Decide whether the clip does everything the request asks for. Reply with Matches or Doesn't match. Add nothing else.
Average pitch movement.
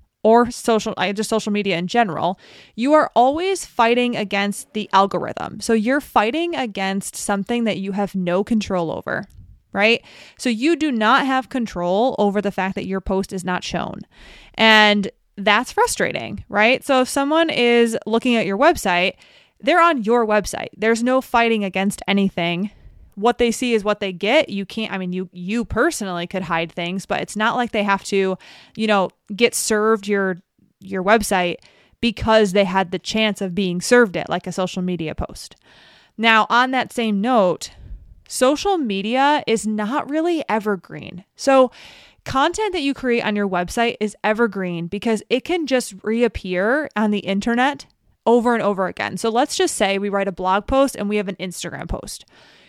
Matches